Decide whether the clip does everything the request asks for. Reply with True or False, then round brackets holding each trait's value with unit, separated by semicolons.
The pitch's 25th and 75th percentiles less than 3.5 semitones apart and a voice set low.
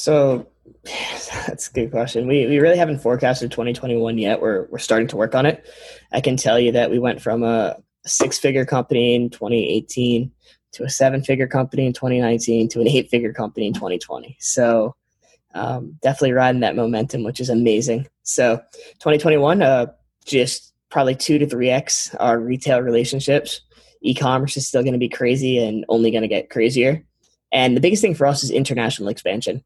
True (2.8 semitones; 125 Hz)